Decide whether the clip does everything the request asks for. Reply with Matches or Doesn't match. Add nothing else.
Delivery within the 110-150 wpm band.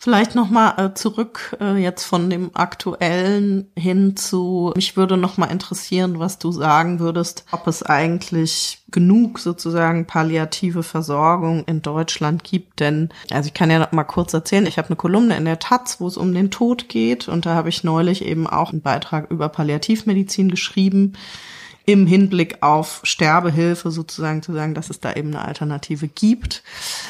Doesn't match